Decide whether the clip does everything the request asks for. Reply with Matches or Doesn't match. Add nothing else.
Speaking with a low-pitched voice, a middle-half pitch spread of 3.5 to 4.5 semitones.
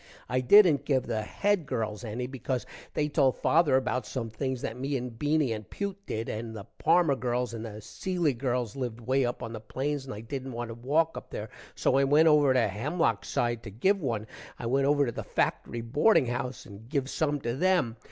Matches